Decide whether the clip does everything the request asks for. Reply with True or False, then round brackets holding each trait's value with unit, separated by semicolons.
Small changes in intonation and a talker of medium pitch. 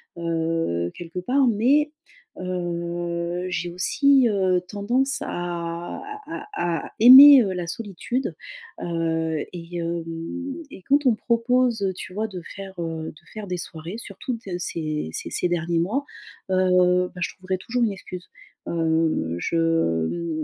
False (4.3 semitones; 180 Hz)